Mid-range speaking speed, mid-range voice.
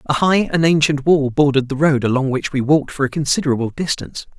No: fast, 220 wpm; medium, 145 Hz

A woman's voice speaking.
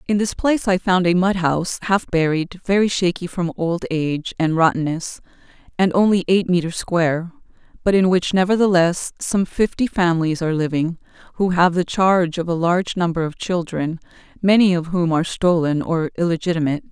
Yes: female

